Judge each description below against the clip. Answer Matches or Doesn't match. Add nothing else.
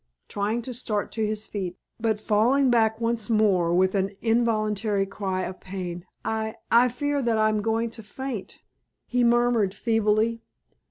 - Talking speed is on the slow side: Doesn't match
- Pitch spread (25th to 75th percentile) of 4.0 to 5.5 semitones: Doesn't match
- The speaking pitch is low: Doesn't match